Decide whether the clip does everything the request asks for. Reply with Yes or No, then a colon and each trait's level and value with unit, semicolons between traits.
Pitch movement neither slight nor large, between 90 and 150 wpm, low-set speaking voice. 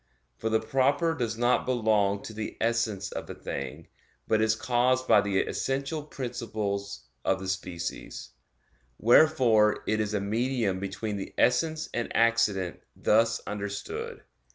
Yes: average, 3.6 semitones; average, 140 wpm; low, 110 Hz